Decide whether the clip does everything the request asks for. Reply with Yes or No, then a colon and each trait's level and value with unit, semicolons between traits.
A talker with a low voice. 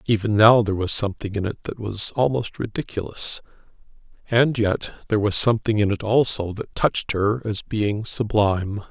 Yes: low, 105 Hz